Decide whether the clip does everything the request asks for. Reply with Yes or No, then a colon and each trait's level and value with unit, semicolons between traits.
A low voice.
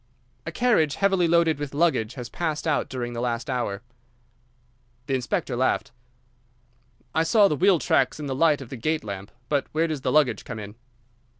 No: medium, 145 Hz